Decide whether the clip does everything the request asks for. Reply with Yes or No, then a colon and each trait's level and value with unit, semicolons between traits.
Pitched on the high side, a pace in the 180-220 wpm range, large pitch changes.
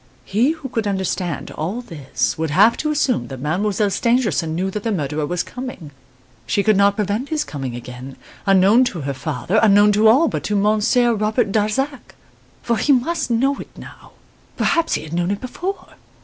Yes: high, 210 Hz; average, 185 wpm; wide, 6.2 semitones